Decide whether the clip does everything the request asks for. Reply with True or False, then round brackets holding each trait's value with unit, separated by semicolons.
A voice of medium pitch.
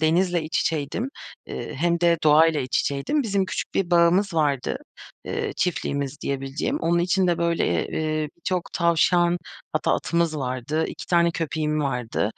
True (165 Hz)